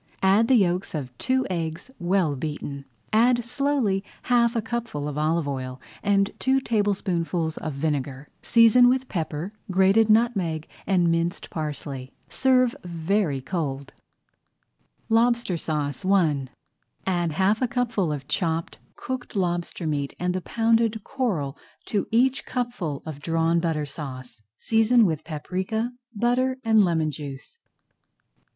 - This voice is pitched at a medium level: Yes, medium, 180 Hz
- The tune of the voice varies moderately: No, wide, 6.8 semitones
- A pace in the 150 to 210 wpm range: No, slow, 135 wpm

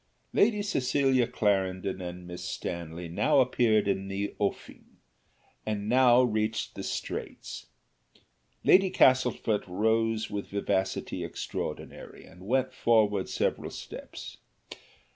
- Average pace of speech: No, slow, 105 wpm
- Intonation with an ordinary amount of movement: Yes, average, 4.6 semitones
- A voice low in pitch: Yes, low, 110 Hz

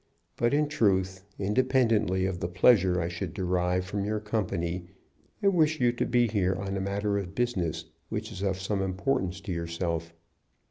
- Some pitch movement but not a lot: Yes, average, 3.8 semitones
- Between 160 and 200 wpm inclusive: Yes, average, 175 wpm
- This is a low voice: Yes, very low, 95 Hz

